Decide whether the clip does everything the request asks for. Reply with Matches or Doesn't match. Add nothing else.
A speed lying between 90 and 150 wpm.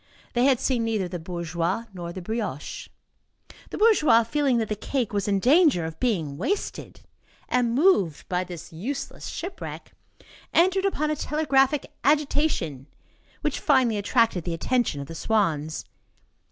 Matches